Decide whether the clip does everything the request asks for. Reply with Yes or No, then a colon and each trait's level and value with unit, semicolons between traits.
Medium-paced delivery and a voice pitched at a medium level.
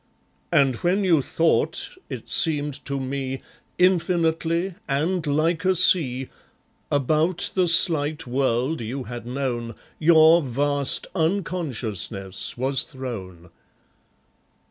No: slow, 100 wpm; medium, 145 Hz